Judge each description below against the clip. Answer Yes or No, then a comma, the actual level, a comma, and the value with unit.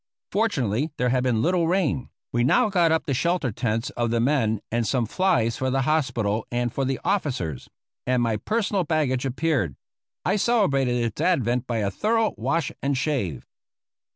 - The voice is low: Yes, low, 130 Hz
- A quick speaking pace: No, average, 175 wpm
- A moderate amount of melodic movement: No, wide, 5.9 semitones